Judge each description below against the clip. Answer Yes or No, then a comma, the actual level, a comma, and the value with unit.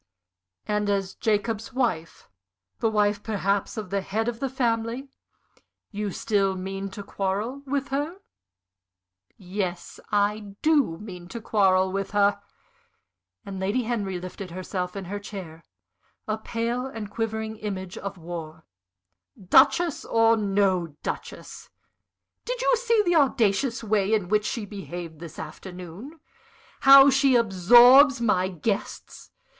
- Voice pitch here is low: No, high, 205 Hz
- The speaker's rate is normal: No, slow, 130 wpm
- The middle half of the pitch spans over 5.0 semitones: No, average, 3.7 semitones